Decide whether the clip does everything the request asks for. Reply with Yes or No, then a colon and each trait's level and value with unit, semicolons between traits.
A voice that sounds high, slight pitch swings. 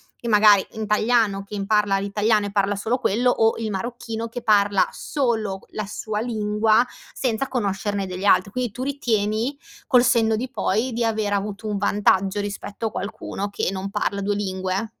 Yes: high, 210 Hz; narrow, 2.2 semitones